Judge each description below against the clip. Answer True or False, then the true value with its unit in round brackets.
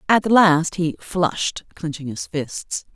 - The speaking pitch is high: False (160 Hz)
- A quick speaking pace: False (160 wpm)